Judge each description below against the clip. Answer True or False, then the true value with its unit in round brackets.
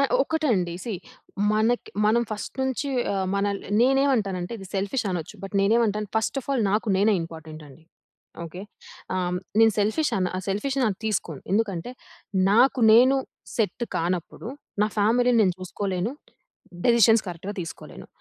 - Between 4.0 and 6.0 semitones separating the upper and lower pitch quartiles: True (4.3 semitones)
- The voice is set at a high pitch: True (210 Hz)